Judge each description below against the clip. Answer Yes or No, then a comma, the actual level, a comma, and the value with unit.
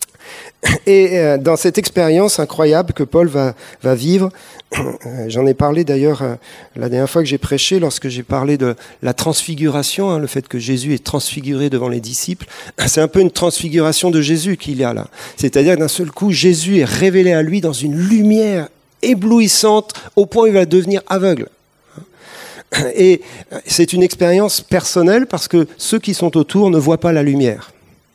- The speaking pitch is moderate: Yes, medium, 165 Hz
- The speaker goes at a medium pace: Yes, average, 185 wpm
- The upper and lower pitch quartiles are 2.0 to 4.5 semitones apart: No, average, 5.2 semitones